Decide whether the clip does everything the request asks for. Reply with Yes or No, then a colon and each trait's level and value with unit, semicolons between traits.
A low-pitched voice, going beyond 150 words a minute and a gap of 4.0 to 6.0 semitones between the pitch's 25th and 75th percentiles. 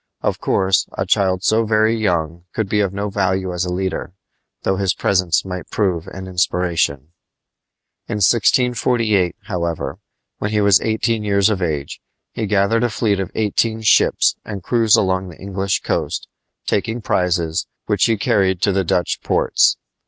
No: very low, 95 Hz; average, 160 wpm; average, 2.9 semitones